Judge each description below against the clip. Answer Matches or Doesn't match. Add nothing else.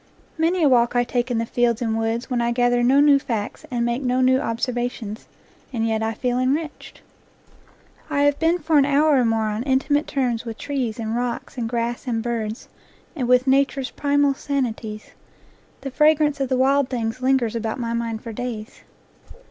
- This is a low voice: Doesn't match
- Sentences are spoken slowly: Doesn't match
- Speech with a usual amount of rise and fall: Matches